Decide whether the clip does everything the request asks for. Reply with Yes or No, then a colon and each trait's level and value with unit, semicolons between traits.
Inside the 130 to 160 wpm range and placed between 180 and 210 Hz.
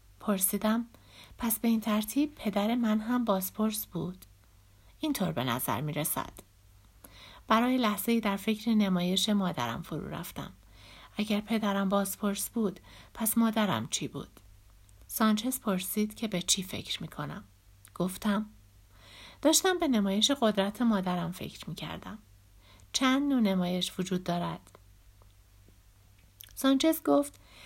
No: average, 120 wpm; high, 190 Hz